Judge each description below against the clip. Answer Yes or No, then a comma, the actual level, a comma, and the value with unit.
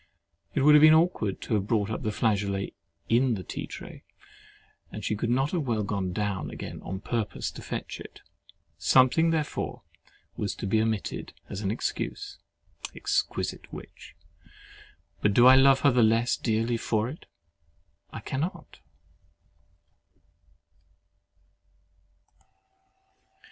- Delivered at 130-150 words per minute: Yes, slow, 135 wpm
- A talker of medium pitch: No, low, 115 Hz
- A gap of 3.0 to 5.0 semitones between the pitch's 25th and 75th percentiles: Yes, average, 4.4 semitones